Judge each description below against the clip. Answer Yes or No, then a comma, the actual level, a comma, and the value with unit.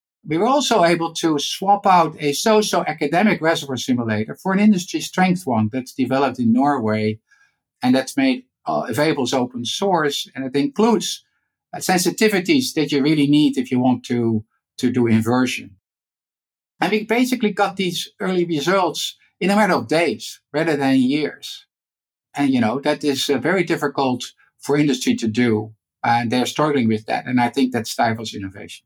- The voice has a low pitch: No, medium, 145 Hz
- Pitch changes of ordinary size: No, wide, 6.8 semitones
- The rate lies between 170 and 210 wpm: Yes, average, 175 wpm